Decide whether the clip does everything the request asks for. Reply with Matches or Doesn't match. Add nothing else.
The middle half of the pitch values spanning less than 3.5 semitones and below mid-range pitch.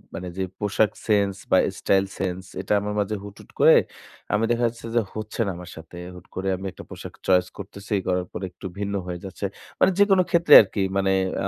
Matches